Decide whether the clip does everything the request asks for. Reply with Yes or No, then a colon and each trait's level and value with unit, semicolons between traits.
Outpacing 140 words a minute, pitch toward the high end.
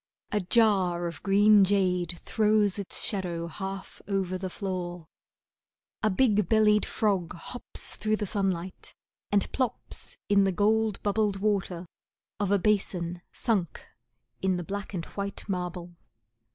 No: slow, 135 wpm; high, 195 Hz